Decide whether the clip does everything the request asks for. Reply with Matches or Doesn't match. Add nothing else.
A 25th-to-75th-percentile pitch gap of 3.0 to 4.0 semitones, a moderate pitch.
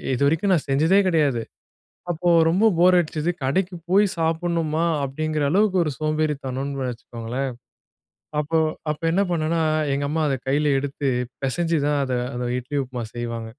Matches